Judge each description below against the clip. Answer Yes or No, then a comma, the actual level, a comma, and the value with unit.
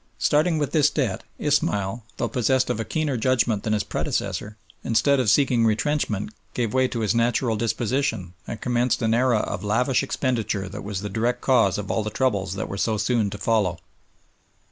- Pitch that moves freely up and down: No, average, 3.7 semitones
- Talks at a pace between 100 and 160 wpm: No, average, 190 wpm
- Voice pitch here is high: No, low, 115 Hz